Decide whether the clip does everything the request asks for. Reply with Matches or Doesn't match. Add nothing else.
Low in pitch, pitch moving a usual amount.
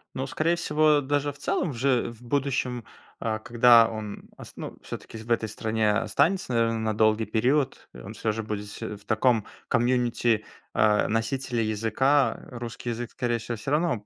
Matches